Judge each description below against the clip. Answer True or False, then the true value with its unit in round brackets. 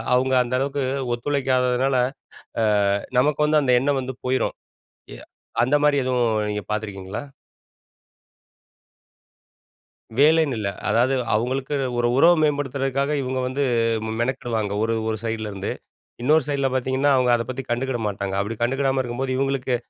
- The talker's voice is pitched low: True (130 Hz)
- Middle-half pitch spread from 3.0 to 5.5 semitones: False (2.6 semitones)